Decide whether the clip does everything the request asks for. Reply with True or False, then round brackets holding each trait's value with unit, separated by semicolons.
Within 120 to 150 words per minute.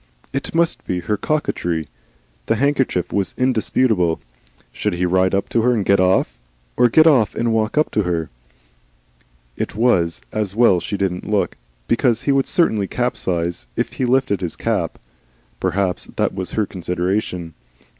False (160 wpm)